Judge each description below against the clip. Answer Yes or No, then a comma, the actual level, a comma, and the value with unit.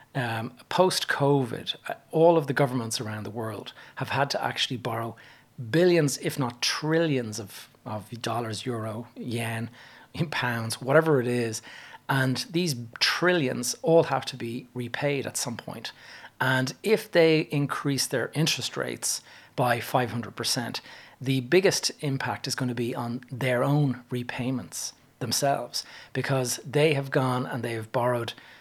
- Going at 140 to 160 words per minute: Yes, average, 145 wpm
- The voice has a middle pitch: No, low, 130 Hz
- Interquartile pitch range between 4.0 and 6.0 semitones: No, average, 3.0 semitones